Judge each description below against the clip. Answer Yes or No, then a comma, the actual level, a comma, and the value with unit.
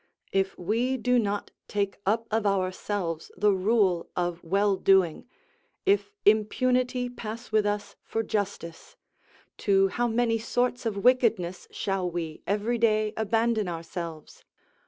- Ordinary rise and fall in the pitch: Yes, average, 3.6 semitones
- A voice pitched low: No, high, 205 Hz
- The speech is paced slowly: Yes, slow, 130 wpm